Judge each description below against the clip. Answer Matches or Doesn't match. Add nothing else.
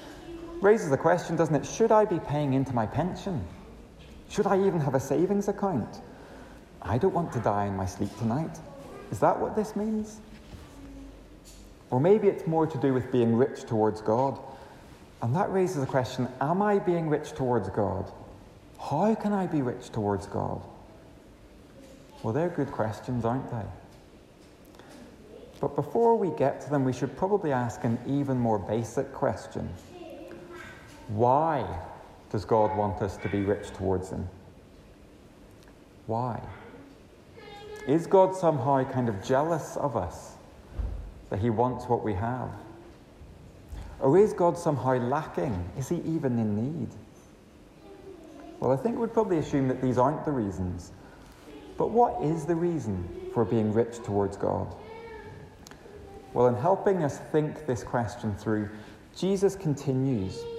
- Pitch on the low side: Matches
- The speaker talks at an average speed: Matches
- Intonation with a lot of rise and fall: Matches